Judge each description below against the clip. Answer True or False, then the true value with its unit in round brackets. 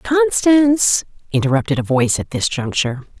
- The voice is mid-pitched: True (165 Hz)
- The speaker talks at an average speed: False (130 wpm)